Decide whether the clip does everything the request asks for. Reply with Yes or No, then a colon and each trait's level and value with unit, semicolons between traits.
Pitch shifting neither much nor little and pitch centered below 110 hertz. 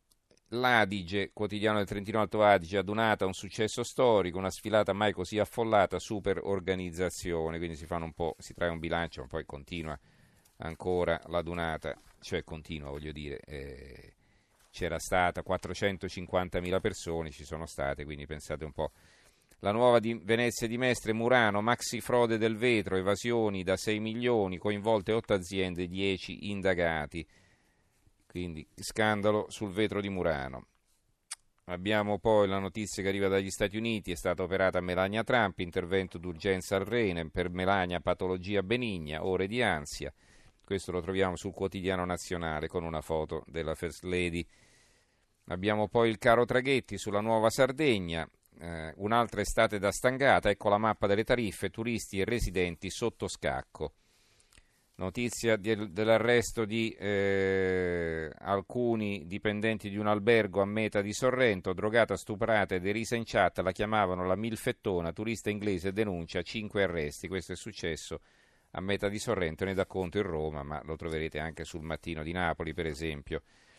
Yes: average, 3.6 semitones; very low, 95 Hz